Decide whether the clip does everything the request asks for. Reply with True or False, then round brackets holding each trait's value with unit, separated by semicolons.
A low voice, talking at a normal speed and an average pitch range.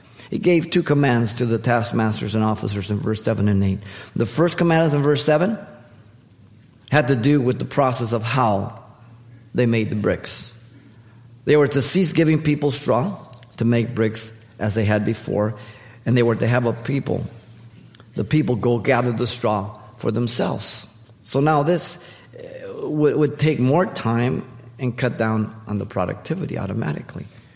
True (120 Hz; 165 wpm; 4.0 semitones)